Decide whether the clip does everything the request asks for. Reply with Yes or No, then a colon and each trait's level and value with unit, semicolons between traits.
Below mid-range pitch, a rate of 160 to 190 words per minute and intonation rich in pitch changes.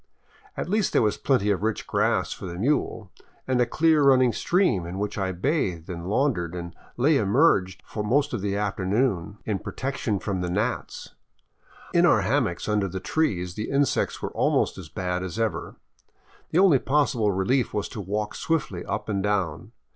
Yes: low, 105 Hz; average, 175 wpm; wide, 6.1 semitones